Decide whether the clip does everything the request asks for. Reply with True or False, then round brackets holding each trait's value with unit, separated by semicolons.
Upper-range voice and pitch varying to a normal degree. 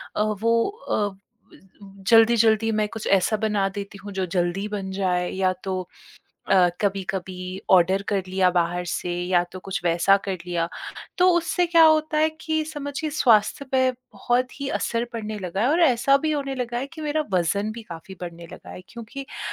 False (210 Hz; 5.8 semitones)